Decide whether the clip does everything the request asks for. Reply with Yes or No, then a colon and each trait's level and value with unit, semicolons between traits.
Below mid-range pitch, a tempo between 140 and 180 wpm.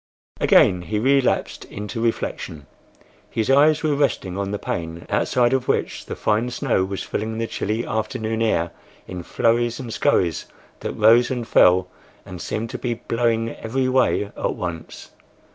Yes: low, 115 Hz; average, 160 wpm